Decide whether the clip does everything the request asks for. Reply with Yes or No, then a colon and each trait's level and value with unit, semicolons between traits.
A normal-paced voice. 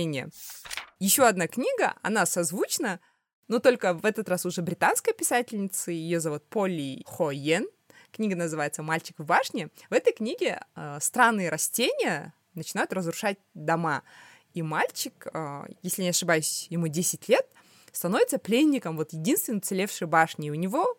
Yes: average, 140 wpm